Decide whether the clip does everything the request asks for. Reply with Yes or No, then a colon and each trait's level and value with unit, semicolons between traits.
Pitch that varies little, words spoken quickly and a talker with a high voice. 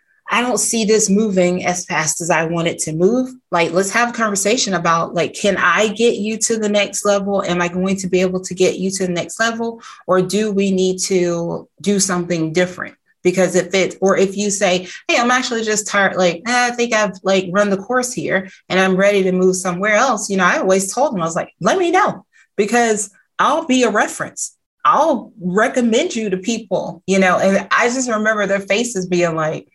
No: average, 3.4 semitones; fast, 220 wpm; high, 195 Hz